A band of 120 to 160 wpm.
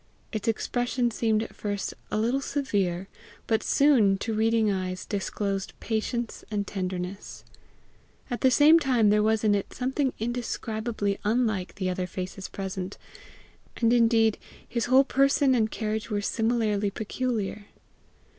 Yes: average, 140 wpm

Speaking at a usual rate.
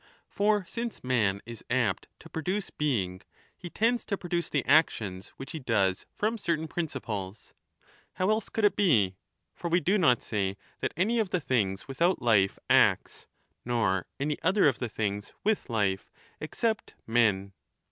Yes: average, 165 wpm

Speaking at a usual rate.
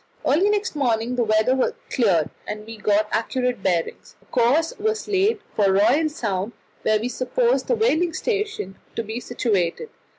Yes: average, 160 wpm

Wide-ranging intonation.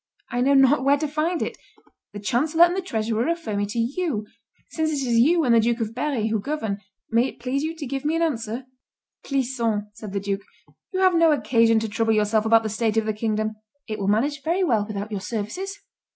Yes: wide, 5.7 semitones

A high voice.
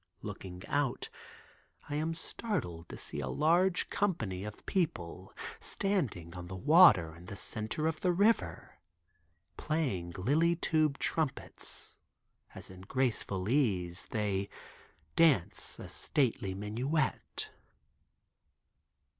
No: low, 125 Hz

